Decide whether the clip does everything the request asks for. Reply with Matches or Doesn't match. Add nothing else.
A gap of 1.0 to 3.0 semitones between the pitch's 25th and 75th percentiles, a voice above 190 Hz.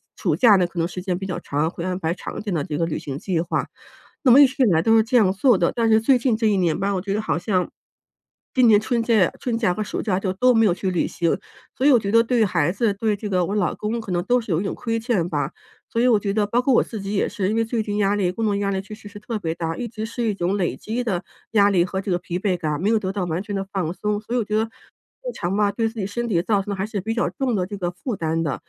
Doesn't match